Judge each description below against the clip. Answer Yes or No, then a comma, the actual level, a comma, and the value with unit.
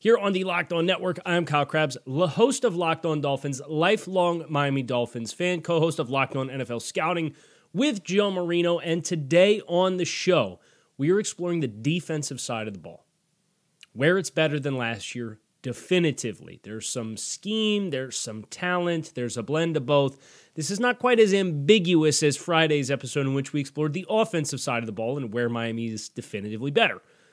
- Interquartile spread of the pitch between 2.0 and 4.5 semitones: No, wide, 5.4 semitones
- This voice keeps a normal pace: Yes, average, 190 wpm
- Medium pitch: Yes, medium, 155 Hz